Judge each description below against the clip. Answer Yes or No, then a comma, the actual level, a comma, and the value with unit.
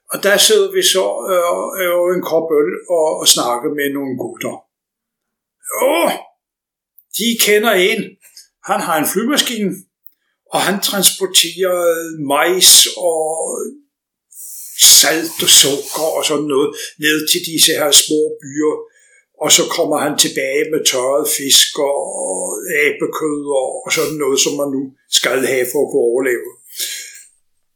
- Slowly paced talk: Yes, slow, 140 wpm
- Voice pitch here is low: No, high, 190 Hz